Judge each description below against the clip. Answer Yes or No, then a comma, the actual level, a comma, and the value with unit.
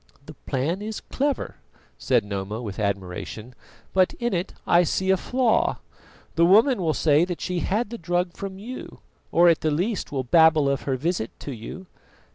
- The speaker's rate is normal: Yes, average, 180 wpm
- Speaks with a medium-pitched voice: Yes, medium, 170 Hz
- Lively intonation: Yes, wide, 5.9 semitones